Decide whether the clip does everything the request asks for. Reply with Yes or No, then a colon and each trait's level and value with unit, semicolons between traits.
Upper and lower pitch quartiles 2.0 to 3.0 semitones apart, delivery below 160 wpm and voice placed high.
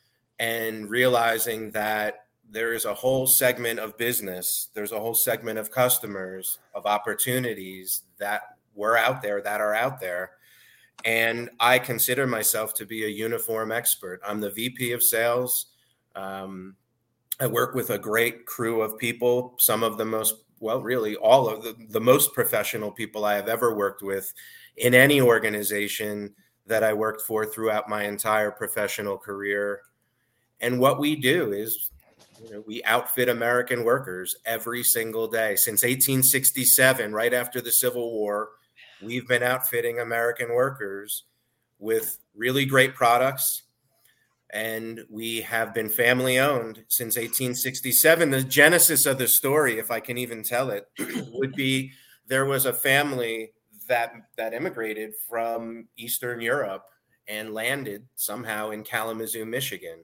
No: narrow, 2.5 semitones; average, 145 wpm; low, 115 Hz